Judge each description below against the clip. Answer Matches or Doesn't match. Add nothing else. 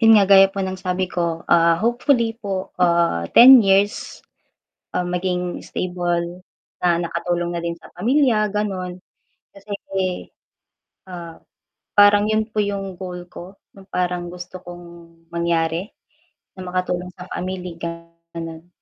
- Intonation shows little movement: Matches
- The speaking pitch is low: Doesn't match